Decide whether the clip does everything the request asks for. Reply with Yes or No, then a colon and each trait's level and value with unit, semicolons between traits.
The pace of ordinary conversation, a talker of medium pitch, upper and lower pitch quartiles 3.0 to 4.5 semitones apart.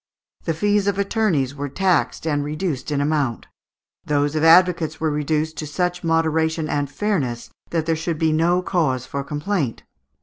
Yes: average, 165 wpm; medium, 160 Hz; average, 3.3 semitones